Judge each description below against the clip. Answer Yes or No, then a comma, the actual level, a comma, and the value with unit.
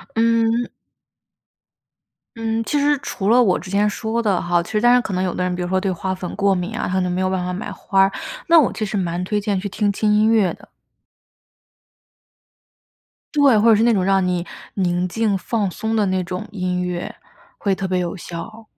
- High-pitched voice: Yes, high, 195 Hz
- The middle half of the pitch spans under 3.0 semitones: No, average, 3.5 semitones